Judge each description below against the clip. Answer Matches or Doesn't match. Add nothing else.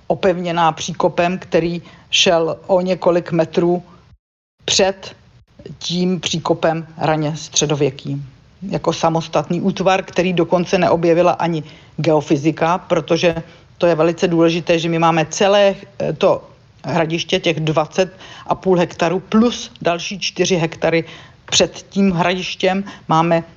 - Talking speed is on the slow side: Matches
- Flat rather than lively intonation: Matches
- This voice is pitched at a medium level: Matches